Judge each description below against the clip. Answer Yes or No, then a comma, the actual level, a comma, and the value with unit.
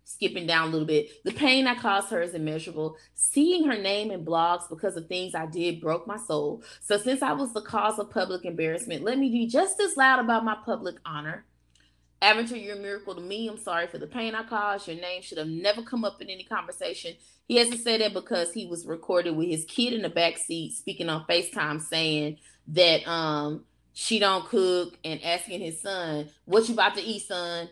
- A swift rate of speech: Yes, fast, 220 wpm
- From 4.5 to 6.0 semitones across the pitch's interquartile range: Yes, average, 5.2 semitones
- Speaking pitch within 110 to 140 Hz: No, medium, 180 Hz